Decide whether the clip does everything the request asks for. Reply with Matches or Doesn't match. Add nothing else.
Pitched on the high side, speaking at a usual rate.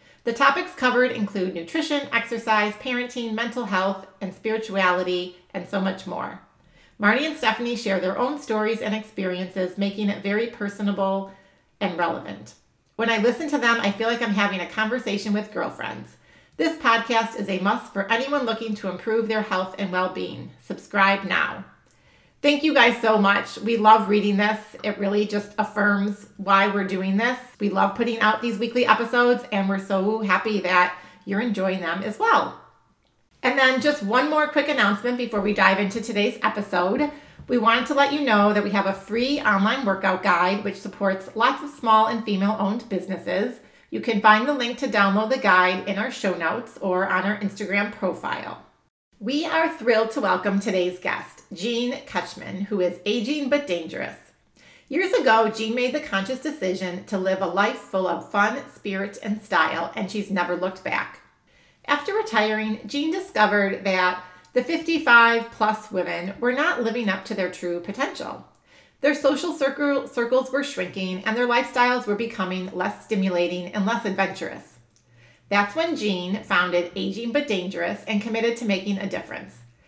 Matches